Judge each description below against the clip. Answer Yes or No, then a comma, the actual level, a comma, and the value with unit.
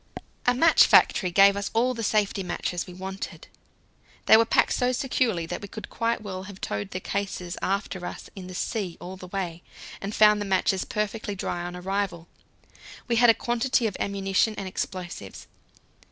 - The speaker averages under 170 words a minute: No, average, 180 wpm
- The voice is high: Yes, high, 200 Hz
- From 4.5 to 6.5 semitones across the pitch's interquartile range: No, average, 3.1 semitones